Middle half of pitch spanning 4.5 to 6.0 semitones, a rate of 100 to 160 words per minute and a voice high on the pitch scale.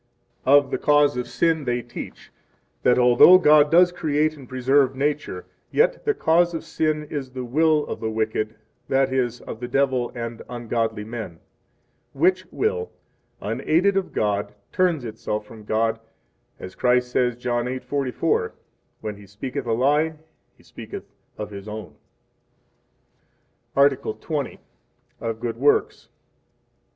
No: average, 4.8 semitones; average, 140 wpm; low, 130 Hz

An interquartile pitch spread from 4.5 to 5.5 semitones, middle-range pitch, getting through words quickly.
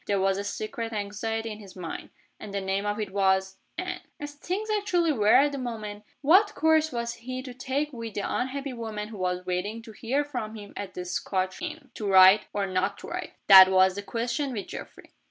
No: average, 5.1 semitones; high, 215 Hz; fast, 215 wpm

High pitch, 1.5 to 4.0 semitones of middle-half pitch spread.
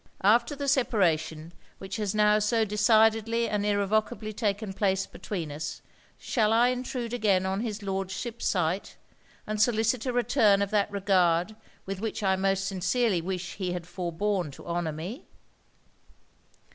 Yes: high, 205 Hz; average, 3.0 semitones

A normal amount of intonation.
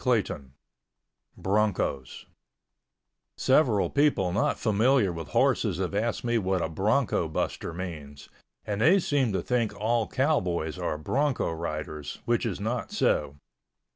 No: wide, 6.3 semitones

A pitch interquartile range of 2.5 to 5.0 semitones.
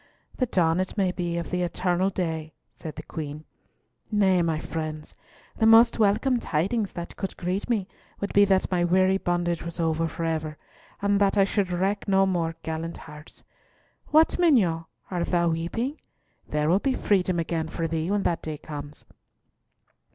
Yes: average, 3.3 semitones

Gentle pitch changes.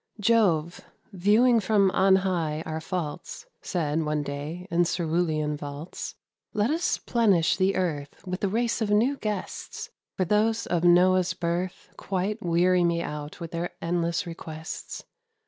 No: average, 3.8 semitones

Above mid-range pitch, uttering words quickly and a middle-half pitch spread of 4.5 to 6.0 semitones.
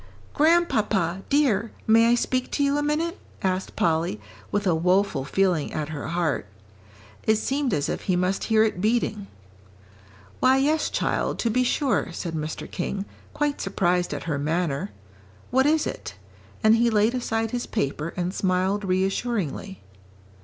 No: high, 200 Hz; average, 155 wpm; wide, 5.5 semitones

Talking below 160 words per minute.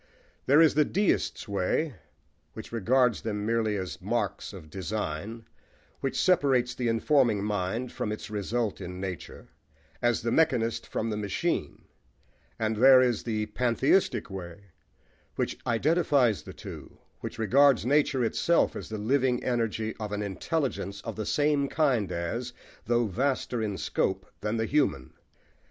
Yes: average, 145 wpm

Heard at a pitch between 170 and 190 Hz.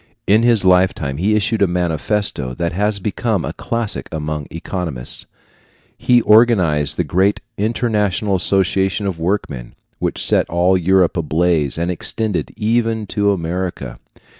No: very low, 95 Hz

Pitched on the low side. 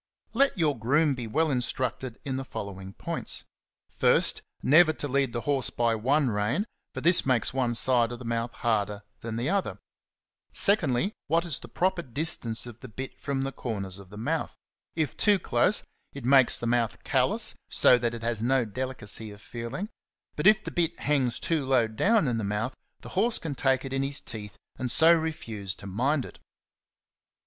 Yes: low, 130 Hz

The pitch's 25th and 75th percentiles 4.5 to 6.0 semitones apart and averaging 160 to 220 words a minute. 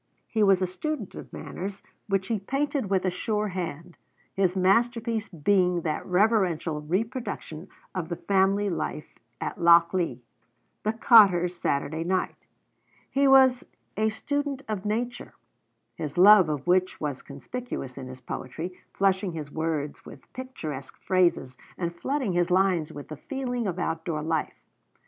No: average, 4.8 semitones; average, 145 wpm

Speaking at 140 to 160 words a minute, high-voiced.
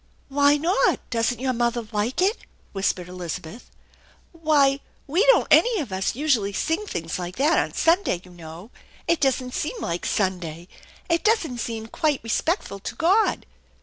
Yes: average, 155 wpm; very high, 250 Hz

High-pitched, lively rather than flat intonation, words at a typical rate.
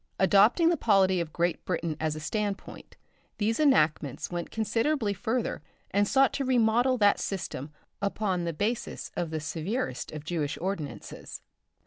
Yes: high, 195 Hz; wide, 5.7 semitones; average, 145 wpm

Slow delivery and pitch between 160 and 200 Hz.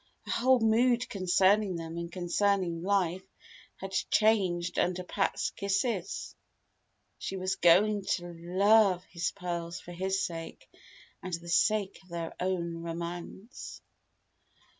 Yes: slow, 120 wpm; medium, 185 Hz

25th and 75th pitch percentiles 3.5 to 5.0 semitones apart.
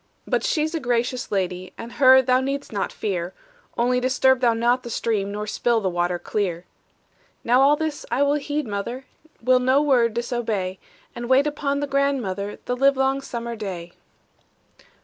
Yes: average, 4.7 semitones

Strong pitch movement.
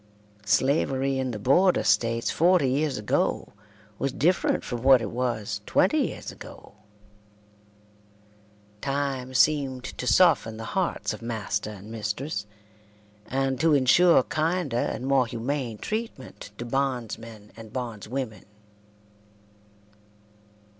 No: average, 3.6 semitones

